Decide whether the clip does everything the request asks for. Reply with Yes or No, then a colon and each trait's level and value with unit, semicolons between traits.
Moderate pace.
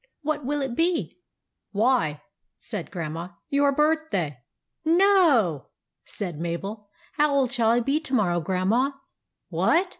Yes: average, 155 wpm